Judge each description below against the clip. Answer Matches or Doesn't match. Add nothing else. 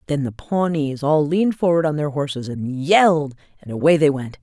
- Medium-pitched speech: Matches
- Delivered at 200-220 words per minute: Matches